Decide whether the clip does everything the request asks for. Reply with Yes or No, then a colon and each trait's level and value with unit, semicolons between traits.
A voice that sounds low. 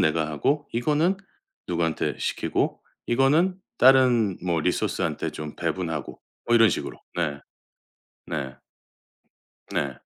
Yes: very low, 95 Hz